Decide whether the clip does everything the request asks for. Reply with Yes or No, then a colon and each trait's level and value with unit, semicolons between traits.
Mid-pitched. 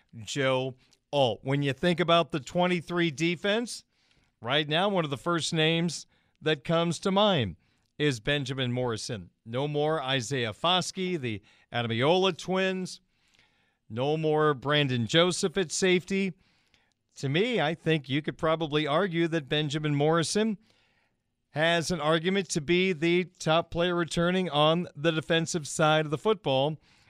Yes: medium, 160 Hz